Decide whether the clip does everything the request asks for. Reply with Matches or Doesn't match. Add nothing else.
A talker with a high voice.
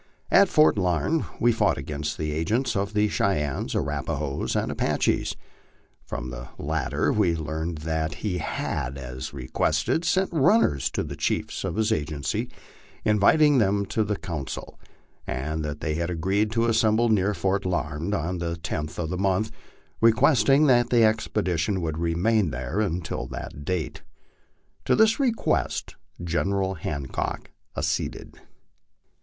Doesn't match